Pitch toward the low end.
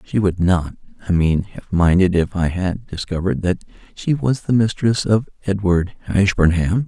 Yes: very low, 95 Hz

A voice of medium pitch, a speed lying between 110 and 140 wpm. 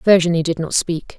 No: medium, 170 Hz; average, 200 wpm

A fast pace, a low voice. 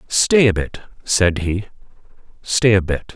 No: average, 150 wpm; low, 100 Hz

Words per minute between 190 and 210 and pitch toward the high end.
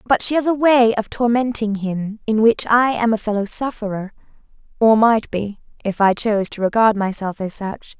Yes: average, 195 wpm; high, 220 Hz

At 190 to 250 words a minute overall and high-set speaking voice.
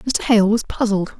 Yes: average, 200 wpm; high, 215 Hz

